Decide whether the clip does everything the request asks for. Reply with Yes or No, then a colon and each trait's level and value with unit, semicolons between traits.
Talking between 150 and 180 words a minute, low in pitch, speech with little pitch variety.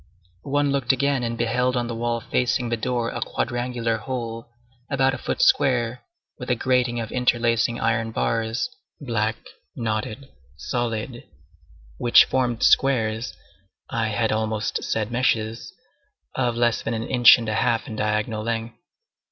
No: average, 140 wpm; low, 120 Hz; narrow, 1.8 semitones